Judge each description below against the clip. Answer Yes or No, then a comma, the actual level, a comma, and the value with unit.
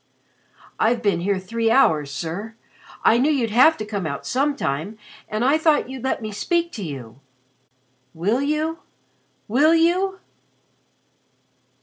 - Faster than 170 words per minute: No, slow, 135 wpm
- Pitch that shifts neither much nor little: No, wide, 7.4 semitones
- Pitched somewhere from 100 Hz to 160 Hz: No, high, 230 Hz